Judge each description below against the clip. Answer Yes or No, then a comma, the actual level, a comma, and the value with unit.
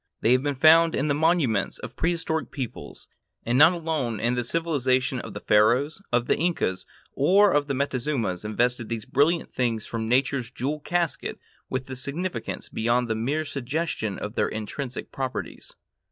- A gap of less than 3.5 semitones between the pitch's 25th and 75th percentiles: No, average, 4.8 semitones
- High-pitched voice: No, low, 130 Hz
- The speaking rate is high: No, average, 165 wpm